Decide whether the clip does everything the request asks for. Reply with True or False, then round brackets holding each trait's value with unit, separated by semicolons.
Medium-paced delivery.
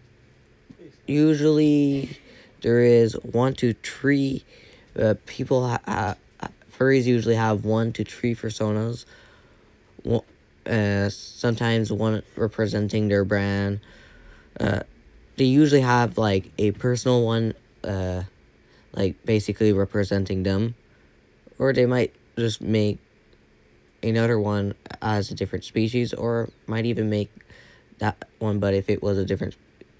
False (120 wpm)